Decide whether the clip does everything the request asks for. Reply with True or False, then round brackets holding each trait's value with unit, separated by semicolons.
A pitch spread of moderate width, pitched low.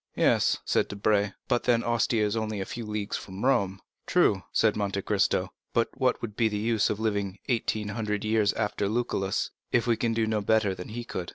False (2.3 semitones; 105 Hz)